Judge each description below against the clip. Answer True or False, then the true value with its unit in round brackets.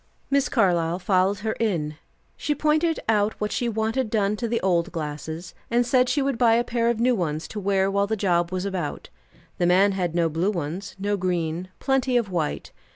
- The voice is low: False (200 Hz)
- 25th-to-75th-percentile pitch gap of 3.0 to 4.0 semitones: False (4.9 semitones)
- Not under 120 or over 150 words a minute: False (205 wpm)